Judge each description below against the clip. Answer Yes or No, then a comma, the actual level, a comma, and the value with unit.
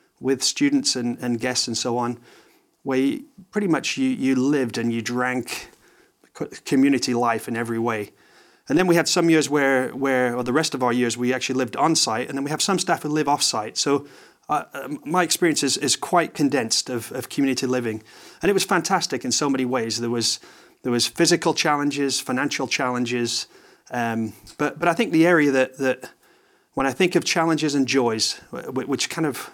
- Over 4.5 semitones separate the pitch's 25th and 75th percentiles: Yes, average, 4.9 semitones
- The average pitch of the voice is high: No, low, 135 Hz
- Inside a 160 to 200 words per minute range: Yes, average, 195 wpm